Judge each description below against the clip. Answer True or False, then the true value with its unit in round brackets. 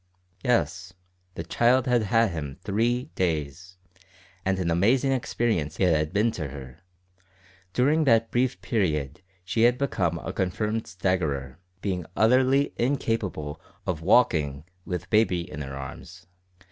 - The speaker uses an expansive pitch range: True (6.9 semitones)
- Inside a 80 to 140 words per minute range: True (135 wpm)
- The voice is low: True (95 Hz)